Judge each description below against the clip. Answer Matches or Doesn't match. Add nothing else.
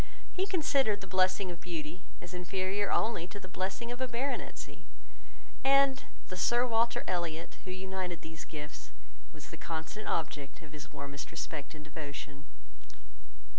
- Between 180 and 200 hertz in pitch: Matches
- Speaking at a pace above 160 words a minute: Doesn't match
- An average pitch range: Doesn't match